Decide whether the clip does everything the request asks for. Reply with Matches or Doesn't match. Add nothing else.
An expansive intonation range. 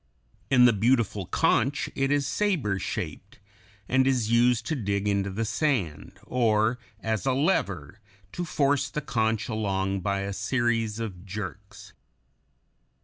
Doesn't match